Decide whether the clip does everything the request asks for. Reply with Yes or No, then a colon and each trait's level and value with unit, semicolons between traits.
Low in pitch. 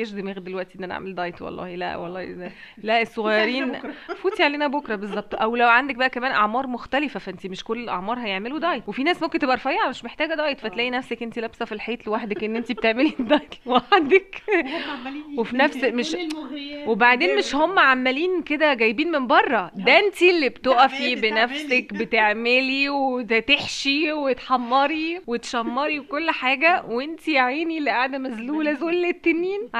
No: very high, 260 Hz